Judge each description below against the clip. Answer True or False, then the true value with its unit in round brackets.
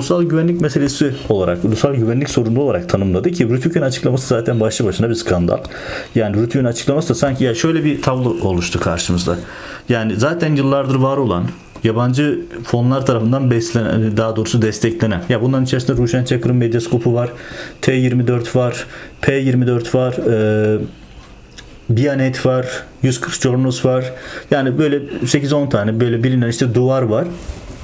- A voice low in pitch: True (125 Hz)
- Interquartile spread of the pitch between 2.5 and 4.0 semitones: True (2.9 semitones)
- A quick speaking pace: True (145 wpm)